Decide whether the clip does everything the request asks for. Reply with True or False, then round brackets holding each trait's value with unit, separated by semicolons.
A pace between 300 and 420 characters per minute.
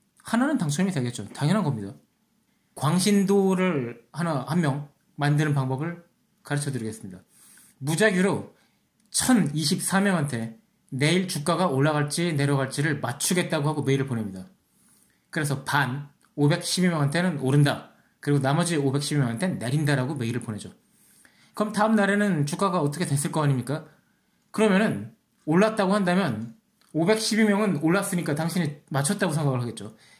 True (310 characters per minute)